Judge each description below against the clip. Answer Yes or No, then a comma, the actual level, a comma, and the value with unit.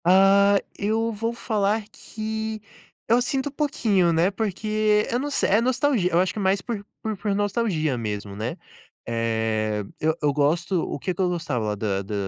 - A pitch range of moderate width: No, wide, 6.5 semitones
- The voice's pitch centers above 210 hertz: No, high, 195 Hz